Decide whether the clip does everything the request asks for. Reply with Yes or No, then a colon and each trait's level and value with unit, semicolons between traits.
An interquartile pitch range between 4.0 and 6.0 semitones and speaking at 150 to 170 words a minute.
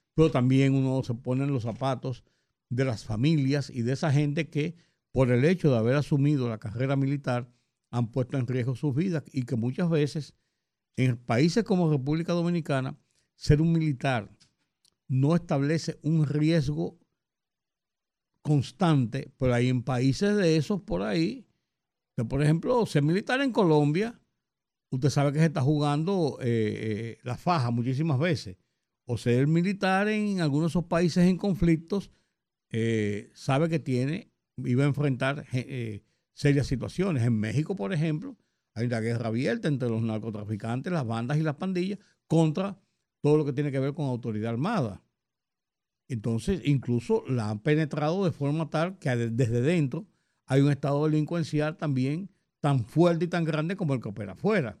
Yes: average, 4.8 semitones; average, 160 wpm